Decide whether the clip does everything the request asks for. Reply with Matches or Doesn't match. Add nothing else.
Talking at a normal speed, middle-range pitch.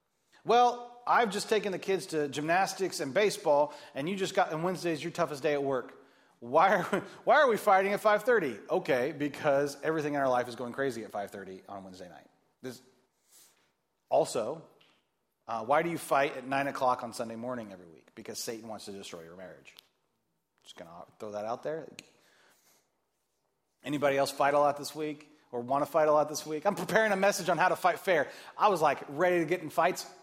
Doesn't match